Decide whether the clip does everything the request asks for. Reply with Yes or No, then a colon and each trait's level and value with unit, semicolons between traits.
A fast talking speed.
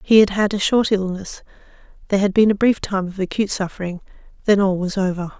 Yes: fast, 210 wpm